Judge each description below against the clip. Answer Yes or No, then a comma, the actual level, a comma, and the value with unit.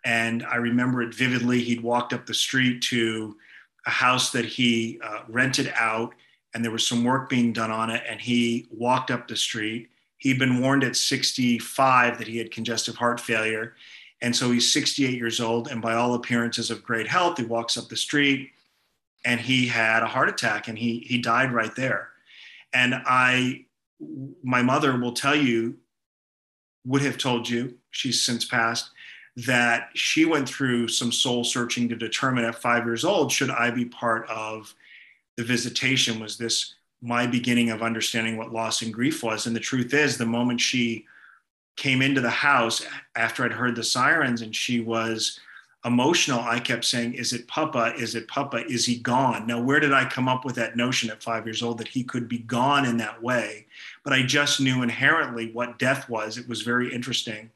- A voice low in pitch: Yes, low, 120 Hz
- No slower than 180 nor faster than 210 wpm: Yes, average, 190 wpm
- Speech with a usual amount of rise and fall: No, narrow, 1.6 semitones